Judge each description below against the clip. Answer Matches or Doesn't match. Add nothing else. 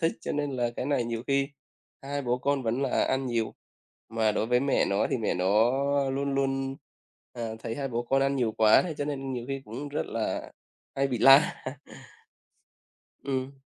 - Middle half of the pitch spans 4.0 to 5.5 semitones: Doesn't match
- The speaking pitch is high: Doesn't match